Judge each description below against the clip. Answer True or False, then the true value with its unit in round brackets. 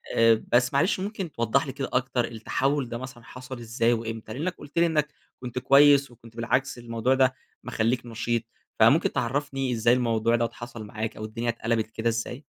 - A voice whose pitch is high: False (120 Hz)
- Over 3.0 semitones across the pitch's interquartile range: False (2.7 semitones)